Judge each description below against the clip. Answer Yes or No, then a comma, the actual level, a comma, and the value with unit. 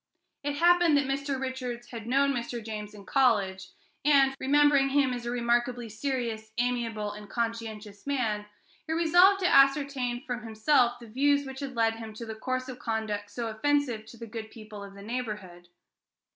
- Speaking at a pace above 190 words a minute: No, average, 175 wpm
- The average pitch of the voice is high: Yes, high, 240 Hz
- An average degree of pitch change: Yes, average, 3.8 semitones